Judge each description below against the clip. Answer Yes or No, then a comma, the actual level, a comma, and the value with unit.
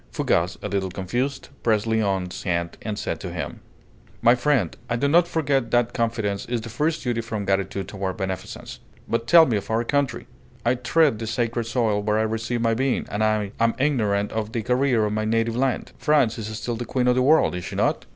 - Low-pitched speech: Yes, low, 115 Hz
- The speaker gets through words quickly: Yes, fast, 215 wpm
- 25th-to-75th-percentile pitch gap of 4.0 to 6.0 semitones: No, average, 3.2 semitones